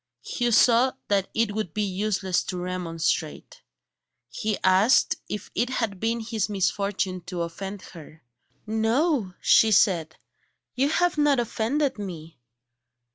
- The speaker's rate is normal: No, slow, 130 wpm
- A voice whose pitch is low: No, high, 205 Hz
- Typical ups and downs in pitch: Yes, average, 4.0 semitones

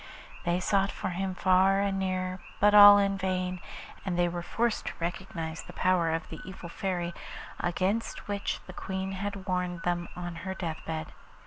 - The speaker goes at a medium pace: Yes, average, 180 wpm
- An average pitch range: No, narrow, 1.8 semitones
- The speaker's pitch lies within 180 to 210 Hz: Yes, medium, 185 Hz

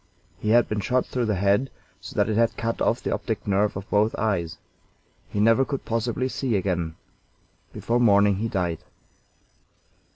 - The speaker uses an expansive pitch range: No, average, 2.8 semitones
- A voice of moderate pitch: No, low, 105 Hz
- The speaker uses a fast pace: No, average, 170 wpm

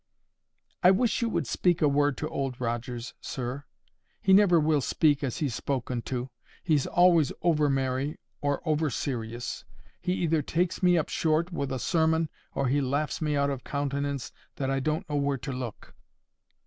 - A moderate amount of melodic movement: Yes, average, 3.4 semitones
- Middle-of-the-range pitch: Yes, medium, 145 Hz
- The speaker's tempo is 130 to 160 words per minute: No, average, 175 wpm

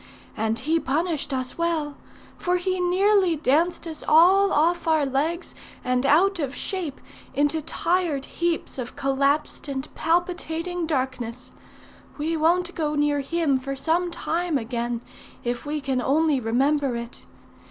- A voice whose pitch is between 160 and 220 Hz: No, very high, 300 Hz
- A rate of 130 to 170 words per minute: Yes, average, 140 wpm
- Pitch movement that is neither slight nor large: Yes, average, 4.1 semitones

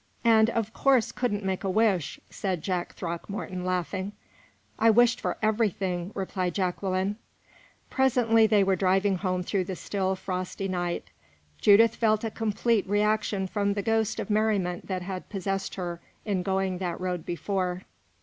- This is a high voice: Yes, high, 195 Hz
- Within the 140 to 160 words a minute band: Yes, average, 150 wpm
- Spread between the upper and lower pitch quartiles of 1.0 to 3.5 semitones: Yes, average, 2.8 semitones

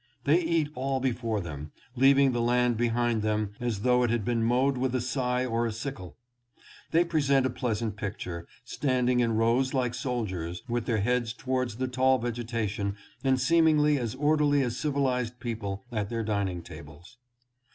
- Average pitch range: Yes, average, 3.0 semitones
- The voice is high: No, low, 120 Hz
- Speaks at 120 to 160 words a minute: No, average, 170 wpm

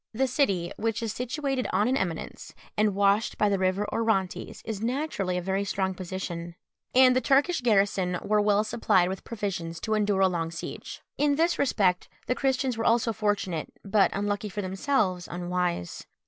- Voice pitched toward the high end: Yes, high, 205 Hz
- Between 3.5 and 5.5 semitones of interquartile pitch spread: Yes, average, 3.8 semitones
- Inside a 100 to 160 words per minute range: No, average, 175 wpm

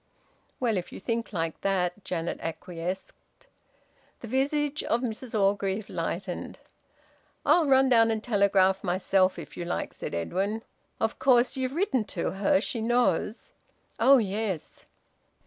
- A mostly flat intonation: No, average, 4.8 semitones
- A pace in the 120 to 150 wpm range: Yes, average, 140 wpm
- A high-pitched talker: Yes, high, 210 Hz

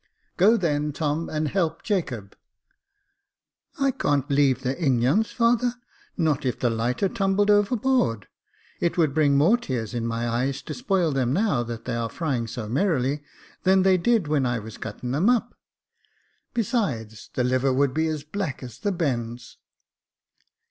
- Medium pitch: Yes, medium, 145 Hz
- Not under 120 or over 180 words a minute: Yes, average, 160 wpm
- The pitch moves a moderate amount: No, wide, 7.7 semitones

